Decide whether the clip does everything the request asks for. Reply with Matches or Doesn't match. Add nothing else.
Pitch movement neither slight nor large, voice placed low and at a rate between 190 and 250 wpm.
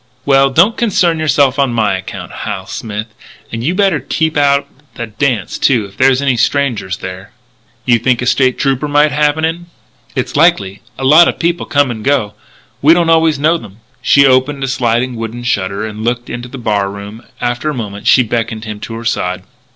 Matches